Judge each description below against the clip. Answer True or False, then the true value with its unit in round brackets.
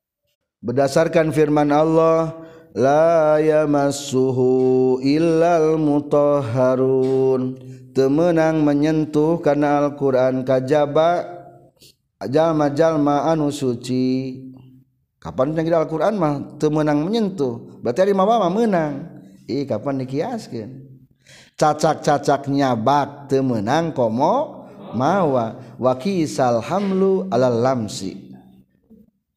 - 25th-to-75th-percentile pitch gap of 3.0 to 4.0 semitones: True (3.7 semitones)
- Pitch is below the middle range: False (145 Hz)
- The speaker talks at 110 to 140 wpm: False (100 wpm)